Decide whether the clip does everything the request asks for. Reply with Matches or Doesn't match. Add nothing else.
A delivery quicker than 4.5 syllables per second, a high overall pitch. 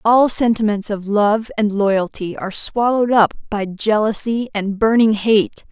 Doesn't match